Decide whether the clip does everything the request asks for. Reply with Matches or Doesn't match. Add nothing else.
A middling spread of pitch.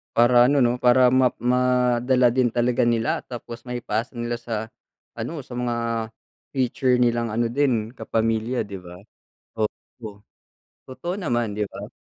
Doesn't match